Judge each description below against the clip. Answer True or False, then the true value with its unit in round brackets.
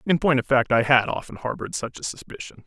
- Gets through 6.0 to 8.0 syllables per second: True (6.3 syllables/s)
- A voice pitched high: False (135 Hz)